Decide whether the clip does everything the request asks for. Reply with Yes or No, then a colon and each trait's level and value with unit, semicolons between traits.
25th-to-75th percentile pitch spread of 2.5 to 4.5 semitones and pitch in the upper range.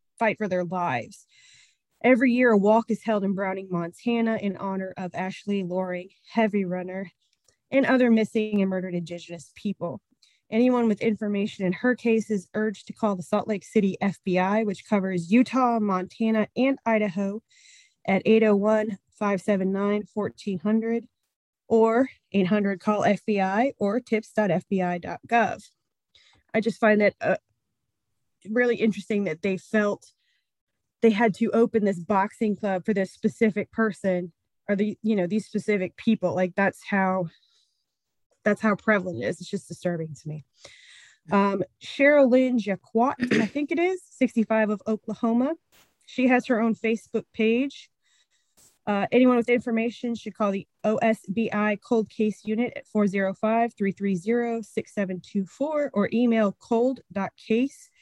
Yes: average, 2.8 semitones; high, 215 Hz